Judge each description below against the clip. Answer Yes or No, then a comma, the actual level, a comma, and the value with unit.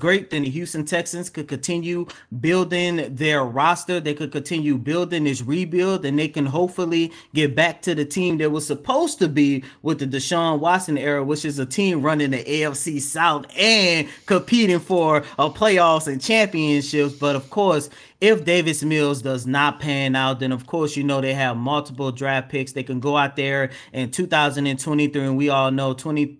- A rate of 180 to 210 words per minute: Yes, average, 185 wpm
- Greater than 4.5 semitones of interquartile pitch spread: No, average, 3.6 semitones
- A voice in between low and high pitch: Yes, medium, 150 Hz